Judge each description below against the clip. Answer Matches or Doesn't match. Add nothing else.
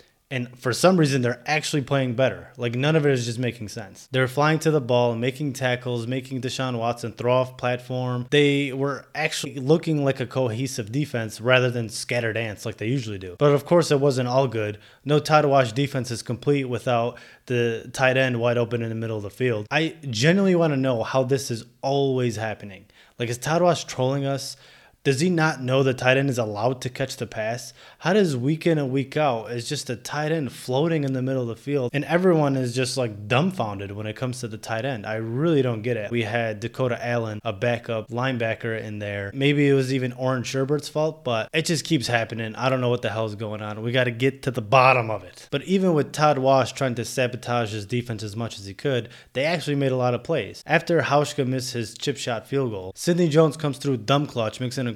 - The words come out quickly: Matches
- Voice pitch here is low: Matches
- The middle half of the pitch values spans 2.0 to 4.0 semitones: Matches